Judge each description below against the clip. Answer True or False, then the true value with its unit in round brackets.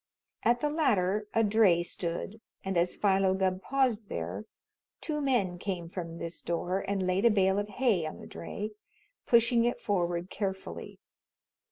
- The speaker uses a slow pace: False (160 wpm)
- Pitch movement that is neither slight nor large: True (4.2 semitones)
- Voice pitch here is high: True (195 Hz)